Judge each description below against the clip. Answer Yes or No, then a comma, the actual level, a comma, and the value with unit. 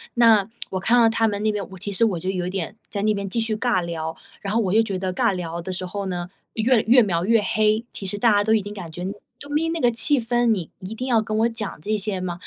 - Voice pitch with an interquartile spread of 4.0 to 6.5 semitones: No, average, 3.5 semitones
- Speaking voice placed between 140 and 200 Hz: No, high, 210 Hz